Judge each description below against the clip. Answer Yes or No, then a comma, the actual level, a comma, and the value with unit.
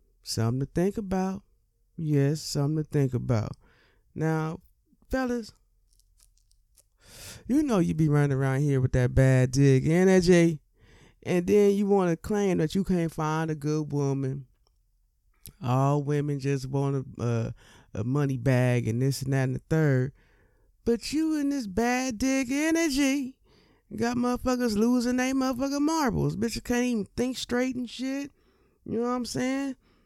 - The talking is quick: No, average, 155 wpm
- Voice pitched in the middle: Yes, medium, 155 Hz